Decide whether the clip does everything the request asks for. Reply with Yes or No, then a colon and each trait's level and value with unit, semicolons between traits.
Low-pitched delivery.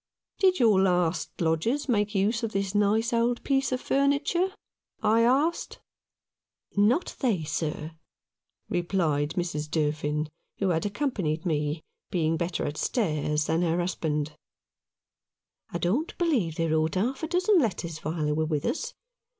No: medium, 180 Hz